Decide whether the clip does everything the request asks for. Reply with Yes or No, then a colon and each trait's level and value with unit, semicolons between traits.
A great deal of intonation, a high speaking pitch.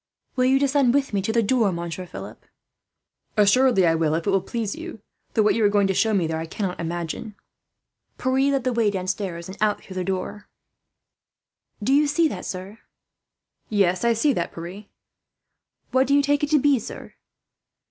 Yes: wide, 5.9 semitones; high, 210 Hz